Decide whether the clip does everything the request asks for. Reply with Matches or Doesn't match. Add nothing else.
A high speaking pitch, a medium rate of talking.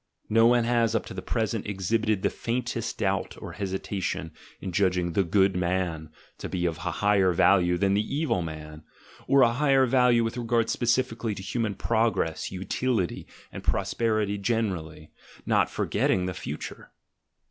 Doesn't match